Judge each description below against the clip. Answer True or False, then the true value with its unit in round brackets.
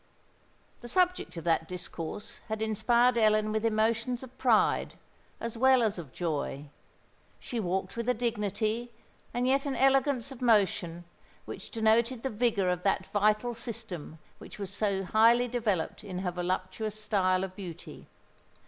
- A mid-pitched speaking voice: False (215 Hz)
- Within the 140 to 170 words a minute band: True (150 wpm)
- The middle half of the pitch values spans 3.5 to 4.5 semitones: True (4.2 semitones)